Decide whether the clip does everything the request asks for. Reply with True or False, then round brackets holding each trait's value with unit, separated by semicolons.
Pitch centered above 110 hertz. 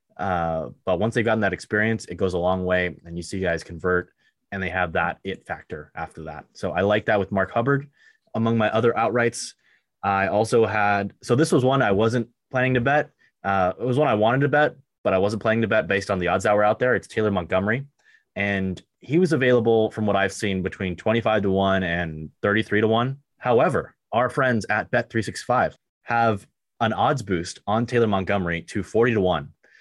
False (105 Hz)